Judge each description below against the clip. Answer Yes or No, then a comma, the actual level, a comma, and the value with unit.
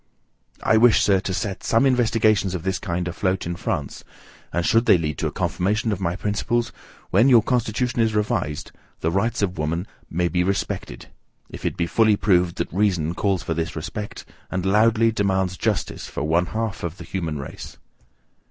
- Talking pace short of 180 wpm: No, average, 185 wpm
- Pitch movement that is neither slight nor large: Yes, average, 4.0 semitones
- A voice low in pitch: Yes, very low, 95 Hz